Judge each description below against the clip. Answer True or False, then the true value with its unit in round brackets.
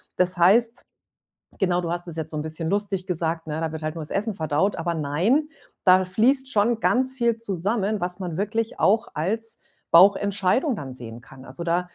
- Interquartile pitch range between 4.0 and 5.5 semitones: True (5.0 semitones)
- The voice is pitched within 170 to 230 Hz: True (185 Hz)